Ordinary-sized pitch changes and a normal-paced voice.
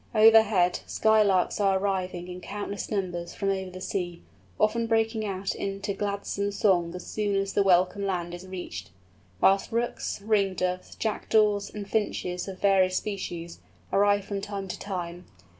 No: narrow, 2.1 semitones; average, 160 wpm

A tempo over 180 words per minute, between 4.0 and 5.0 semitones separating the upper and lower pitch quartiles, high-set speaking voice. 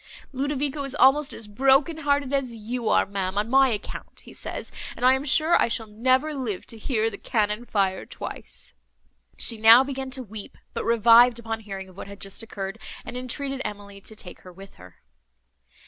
Yes: average, 195 wpm; average, 4.4 semitones; high, 230 Hz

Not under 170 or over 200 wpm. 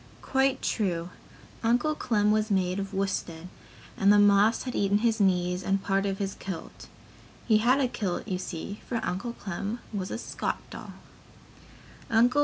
No: average, 160 wpm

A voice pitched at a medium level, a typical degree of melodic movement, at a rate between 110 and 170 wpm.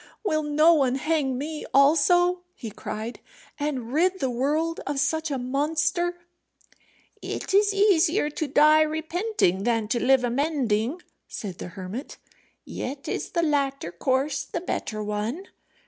No: very high, 290 Hz; average, 4.4 semitones; average, 140 wpm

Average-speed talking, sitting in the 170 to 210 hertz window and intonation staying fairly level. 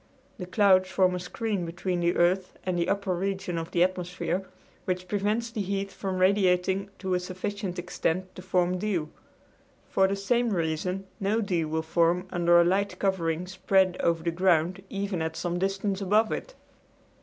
Yes: average, 175 wpm; medium, 185 Hz; narrow, 2.0 semitones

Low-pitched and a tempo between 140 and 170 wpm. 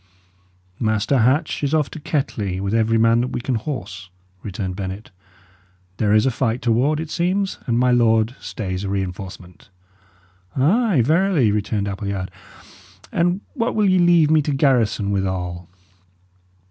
Yes: low, 115 Hz; average, 145 wpm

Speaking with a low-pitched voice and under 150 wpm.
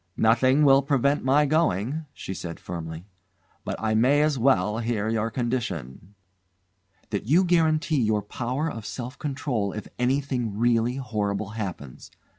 Yes: low, 120 Hz; average, 140 wpm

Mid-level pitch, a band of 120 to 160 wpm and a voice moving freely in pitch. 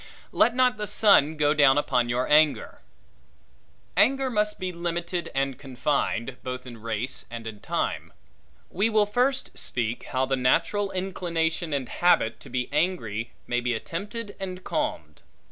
Yes: medium, 155 Hz; average, 150 wpm; wide, 7.8 semitones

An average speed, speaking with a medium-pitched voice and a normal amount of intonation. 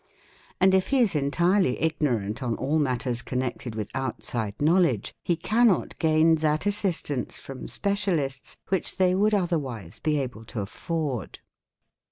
No: average, 155 wpm; medium, 150 Hz; wide, 6.4 semitones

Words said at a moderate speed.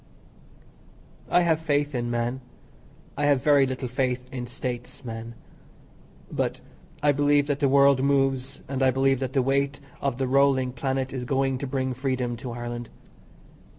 Yes: average, 160 wpm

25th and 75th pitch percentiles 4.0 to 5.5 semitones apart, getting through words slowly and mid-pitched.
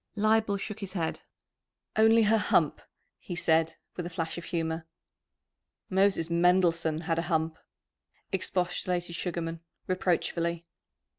No: narrow, 2.6 semitones; slow, 120 wpm; medium, 175 Hz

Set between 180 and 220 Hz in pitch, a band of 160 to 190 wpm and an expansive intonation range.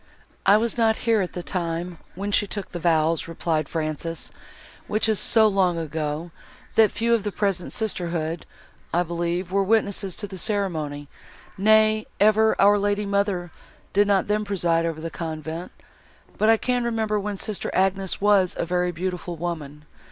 No: high, 190 Hz; average, 165 wpm; average, 3.7 semitones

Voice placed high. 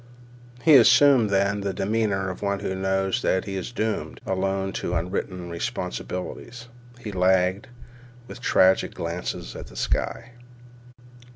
No: very low, 95 Hz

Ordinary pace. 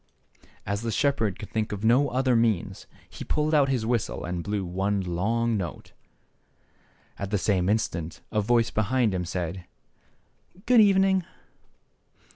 Yes: average, 155 wpm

